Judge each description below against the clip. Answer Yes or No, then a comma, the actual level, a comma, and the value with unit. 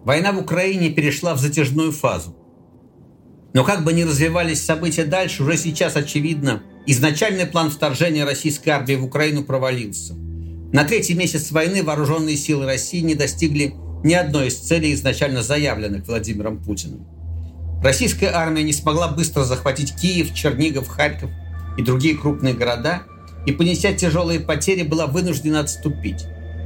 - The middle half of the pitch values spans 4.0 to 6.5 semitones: Yes, average, 4.8 semitones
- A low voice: No, medium, 150 Hz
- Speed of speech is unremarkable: Yes, average, 140 wpm